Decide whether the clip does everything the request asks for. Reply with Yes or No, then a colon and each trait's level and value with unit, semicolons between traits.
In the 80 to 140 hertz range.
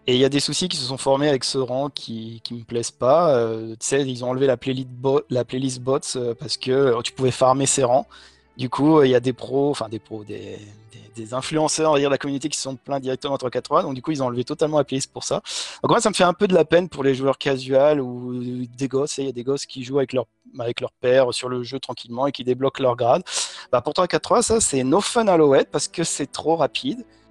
Yes: low, 135 Hz